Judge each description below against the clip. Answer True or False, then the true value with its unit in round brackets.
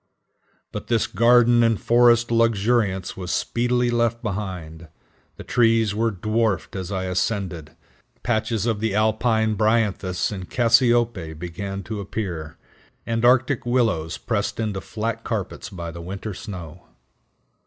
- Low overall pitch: True (110 Hz)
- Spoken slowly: True (130 wpm)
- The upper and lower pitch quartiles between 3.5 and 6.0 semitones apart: True (3.8 semitones)